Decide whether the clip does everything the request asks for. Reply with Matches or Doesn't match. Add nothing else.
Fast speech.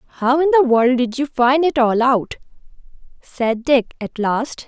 Doesn't match